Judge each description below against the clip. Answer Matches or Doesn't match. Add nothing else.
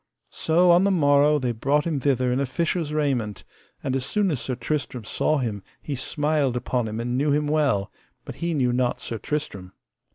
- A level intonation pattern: Doesn't match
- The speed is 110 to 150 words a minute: Doesn't match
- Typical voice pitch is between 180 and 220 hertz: Doesn't match